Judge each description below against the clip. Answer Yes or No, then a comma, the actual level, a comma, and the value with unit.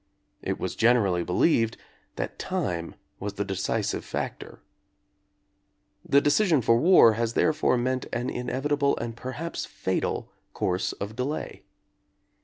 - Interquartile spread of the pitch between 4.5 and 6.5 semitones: Yes, wide, 5.6 semitones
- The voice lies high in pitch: No, low, 120 Hz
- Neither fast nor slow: No, slow, 120 wpm